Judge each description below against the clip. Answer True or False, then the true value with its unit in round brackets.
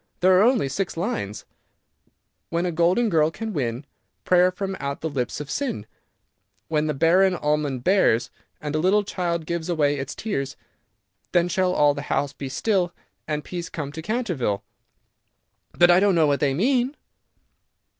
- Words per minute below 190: True (165 wpm)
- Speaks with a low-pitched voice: False (170 Hz)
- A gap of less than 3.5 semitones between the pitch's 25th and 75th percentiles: False (4.5 semitones)